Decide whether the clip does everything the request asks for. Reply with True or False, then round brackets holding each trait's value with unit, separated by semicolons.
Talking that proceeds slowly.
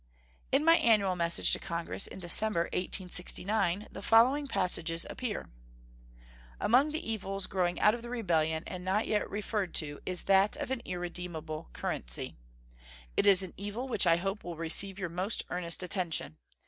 False (160 wpm)